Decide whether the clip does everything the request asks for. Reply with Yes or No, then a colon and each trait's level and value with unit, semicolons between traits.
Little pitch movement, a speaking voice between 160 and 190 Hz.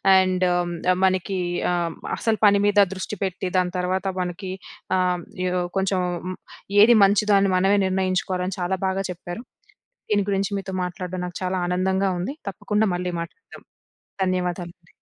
Yes: narrow, 1.5 semitones; medium, 185 Hz